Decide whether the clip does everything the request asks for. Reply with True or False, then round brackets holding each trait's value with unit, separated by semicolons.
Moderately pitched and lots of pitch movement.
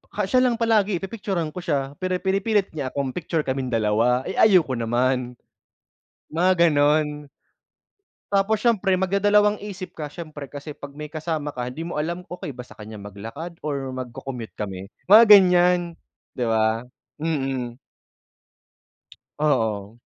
True (150 Hz; 6.5 semitones)